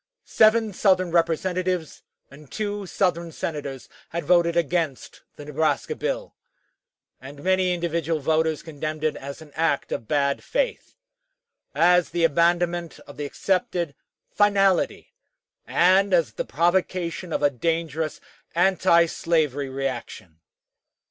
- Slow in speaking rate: Yes, slow, 115 wpm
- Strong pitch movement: No, average, 3.4 semitones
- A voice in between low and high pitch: Yes, medium, 170 Hz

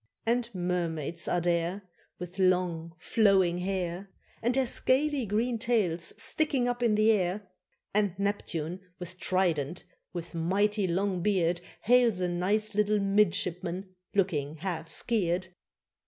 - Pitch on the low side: No, medium, 185 Hz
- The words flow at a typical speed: No, slow, 125 wpm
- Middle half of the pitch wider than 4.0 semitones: No, average, 3.4 semitones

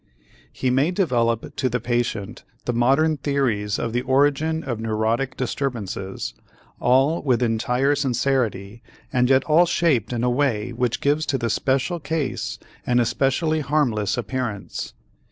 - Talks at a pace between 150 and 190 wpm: No, average, 140 wpm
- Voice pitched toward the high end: No, low, 125 Hz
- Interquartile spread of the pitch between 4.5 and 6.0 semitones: No, average, 3.3 semitones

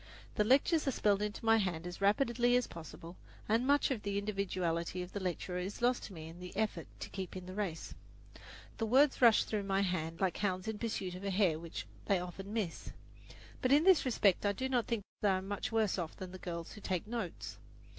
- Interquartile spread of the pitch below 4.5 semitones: Yes, average, 3.7 semitones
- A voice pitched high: Yes, high, 200 Hz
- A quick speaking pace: Yes, fast, 225 wpm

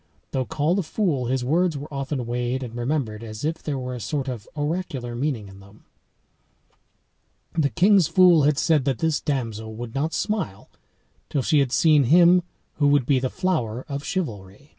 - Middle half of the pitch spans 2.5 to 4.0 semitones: No, average, 4.6 semitones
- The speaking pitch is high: No, medium, 140 Hz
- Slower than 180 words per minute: Yes, average, 170 wpm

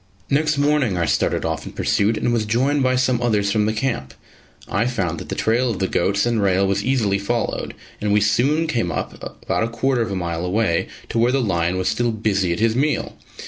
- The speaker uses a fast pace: Yes, fast, 225 wpm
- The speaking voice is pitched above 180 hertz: No, low, 110 Hz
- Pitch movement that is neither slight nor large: Yes, average, 4.2 semitones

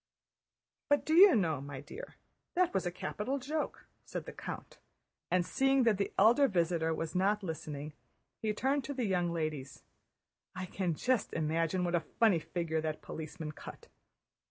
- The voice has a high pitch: No, medium, 180 Hz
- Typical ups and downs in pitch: No, wide, 7.3 semitones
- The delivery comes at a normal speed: Yes, average, 165 wpm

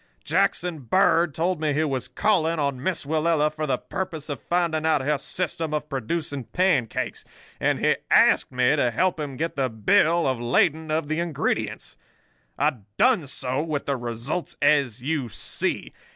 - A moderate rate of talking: Yes, average, 165 wpm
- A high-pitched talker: No, medium, 150 Hz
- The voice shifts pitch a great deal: No, average, 3.7 semitones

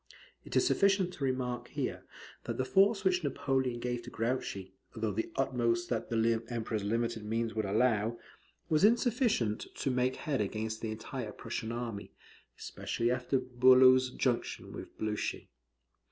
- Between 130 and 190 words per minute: Yes, average, 150 wpm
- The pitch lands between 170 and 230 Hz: No, low, 120 Hz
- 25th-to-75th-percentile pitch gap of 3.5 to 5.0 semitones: No, average, 2.8 semitones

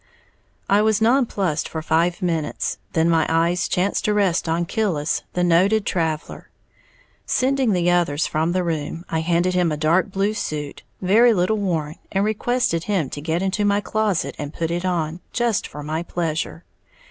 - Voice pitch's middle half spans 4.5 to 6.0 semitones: No, average, 3.9 semitones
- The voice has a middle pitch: Yes, medium, 175 Hz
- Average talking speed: Yes, average, 175 wpm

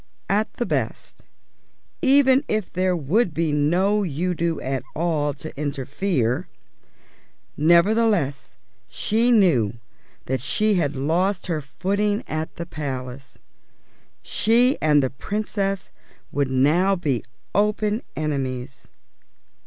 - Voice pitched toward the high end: No, medium, 170 Hz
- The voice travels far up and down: Yes, wide, 6.5 semitones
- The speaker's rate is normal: No, slow, 105 wpm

